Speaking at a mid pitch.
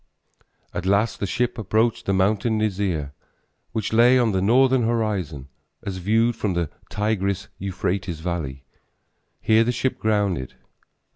No: low, 100 Hz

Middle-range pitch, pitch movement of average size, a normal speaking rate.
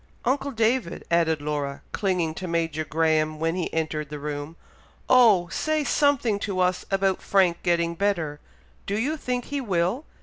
No: medium, 175 Hz; wide, 5.7 semitones; average, 160 wpm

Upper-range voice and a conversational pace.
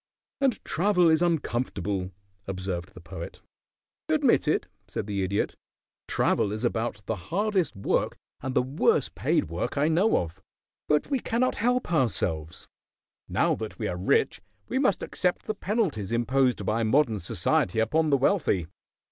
No: low, 125 Hz; average, 150 wpm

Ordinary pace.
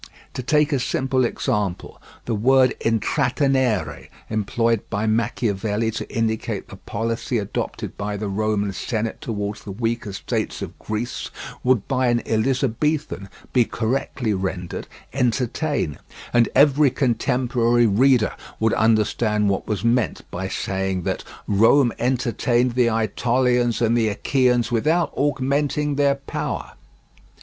No: slow, 125 wpm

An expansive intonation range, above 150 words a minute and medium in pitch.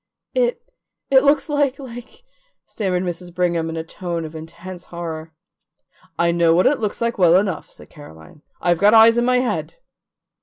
Yes: wide, 6.4 semitones; average, 180 wpm; medium, 180 Hz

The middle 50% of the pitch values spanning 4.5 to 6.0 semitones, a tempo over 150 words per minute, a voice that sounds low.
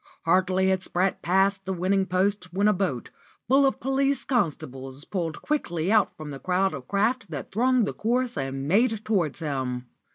No: wide, 5.5 semitones; average, 175 wpm; high, 190 Hz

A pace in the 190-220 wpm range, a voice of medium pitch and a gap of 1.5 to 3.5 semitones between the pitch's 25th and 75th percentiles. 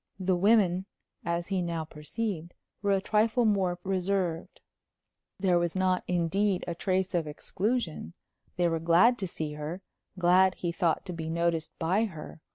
No: average, 160 wpm; medium, 180 Hz; narrow, 2.6 semitones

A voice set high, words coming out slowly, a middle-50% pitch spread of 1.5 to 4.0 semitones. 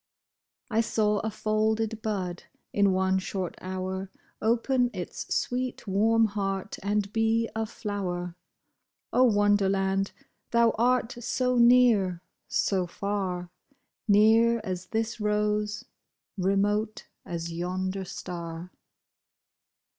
Yes: high, 205 Hz; slow, 100 wpm; average, 2.9 semitones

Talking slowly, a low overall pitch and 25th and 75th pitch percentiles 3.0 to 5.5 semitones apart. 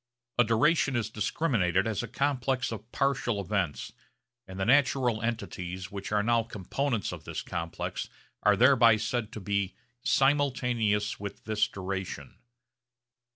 Yes: slow, 130 wpm; low, 110 Hz; average, 3.9 semitones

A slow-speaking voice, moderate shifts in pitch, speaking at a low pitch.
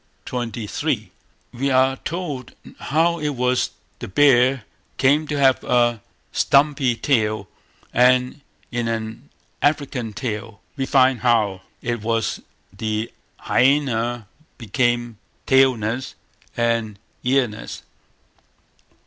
Yes: slow, 100 wpm; average, 3.0 semitones; low, 125 Hz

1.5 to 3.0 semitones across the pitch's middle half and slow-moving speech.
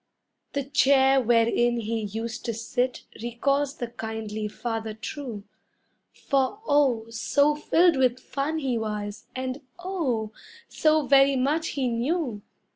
No: average, 3.8 semitones; slow, 125 wpm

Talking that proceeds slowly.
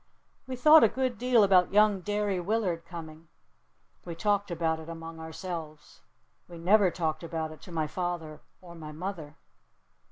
No: average, 160 wpm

